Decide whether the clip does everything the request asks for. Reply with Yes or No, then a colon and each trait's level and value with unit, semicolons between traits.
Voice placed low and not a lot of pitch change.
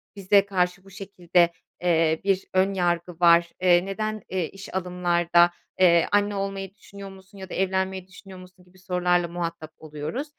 No: medium, 185 Hz; narrow, 1.9 semitones